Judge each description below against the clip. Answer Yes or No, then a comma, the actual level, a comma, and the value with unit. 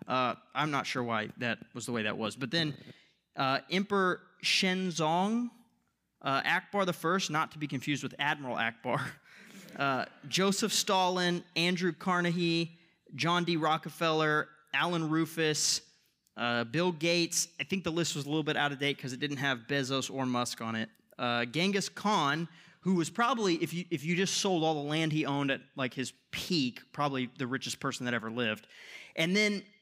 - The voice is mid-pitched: Yes, medium, 160 Hz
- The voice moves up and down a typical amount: Yes, average, 4.3 semitones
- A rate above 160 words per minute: Yes, average, 180 wpm